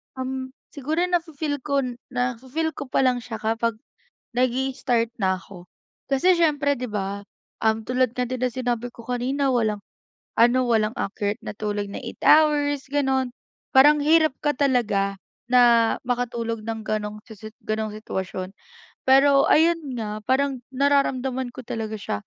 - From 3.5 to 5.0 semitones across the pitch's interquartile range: Yes, average, 3.8 semitones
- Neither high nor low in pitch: No, very high, 250 Hz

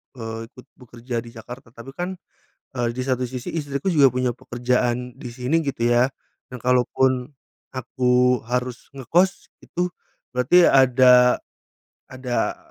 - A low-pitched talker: Yes, low, 125 Hz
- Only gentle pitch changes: Yes, narrow, 1.4 semitones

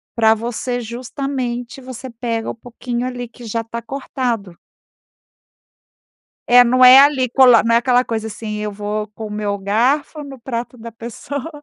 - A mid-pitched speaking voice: No, high, 240 Hz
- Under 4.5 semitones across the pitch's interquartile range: Yes, narrow, 2.4 semitones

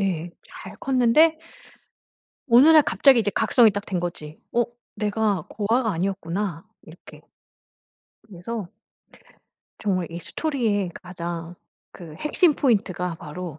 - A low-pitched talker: No, high, 200 Hz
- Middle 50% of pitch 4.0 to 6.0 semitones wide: Yes, average, 5.2 semitones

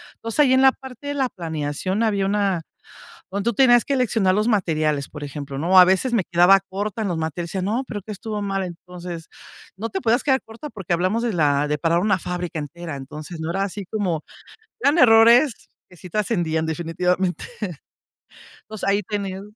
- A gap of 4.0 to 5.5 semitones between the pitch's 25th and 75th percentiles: Yes, average, 4.8 semitones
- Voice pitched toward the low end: No, high, 190 Hz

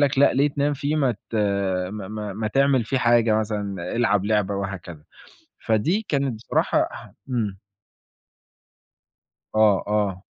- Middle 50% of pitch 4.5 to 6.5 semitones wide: Yes, average, 4.9 semitones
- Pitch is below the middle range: Yes, low, 110 Hz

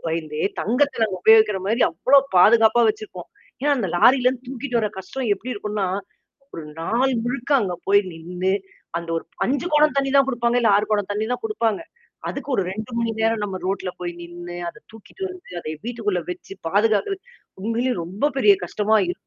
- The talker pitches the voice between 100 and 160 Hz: No, high, 220 Hz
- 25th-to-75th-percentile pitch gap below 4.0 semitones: No, average, 4.6 semitones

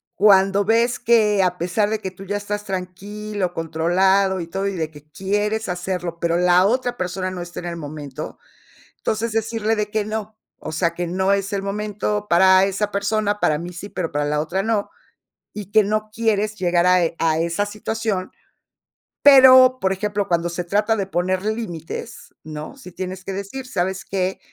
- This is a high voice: Yes, high, 195 Hz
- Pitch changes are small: No, average, 3.1 semitones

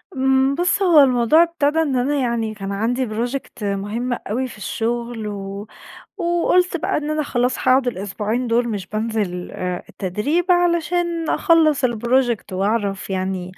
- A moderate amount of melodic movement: No, wide, 6.0 semitones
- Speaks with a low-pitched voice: No, high, 240 Hz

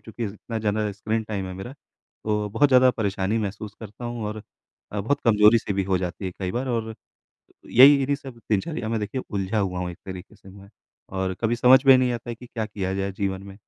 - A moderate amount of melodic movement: Yes, average, 3.4 semitones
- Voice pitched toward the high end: No, low, 105 Hz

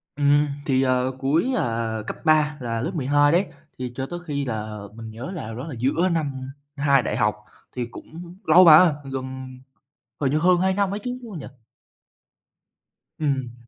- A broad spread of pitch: No, average, 4.5 semitones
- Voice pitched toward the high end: No, medium, 140 Hz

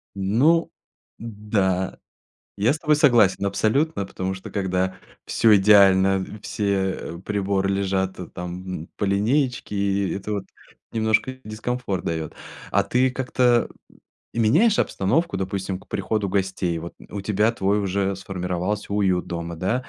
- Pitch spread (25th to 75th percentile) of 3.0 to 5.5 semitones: No, narrow, 2.6 semitones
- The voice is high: No, low, 100 Hz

